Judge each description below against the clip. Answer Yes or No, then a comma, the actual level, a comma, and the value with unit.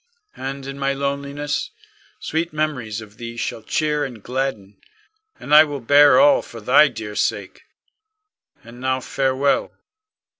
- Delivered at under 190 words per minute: Yes, average, 140 wpm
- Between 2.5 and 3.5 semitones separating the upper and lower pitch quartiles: Yes, average, 3.0 semitones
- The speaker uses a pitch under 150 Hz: Yes, low, 135 Hz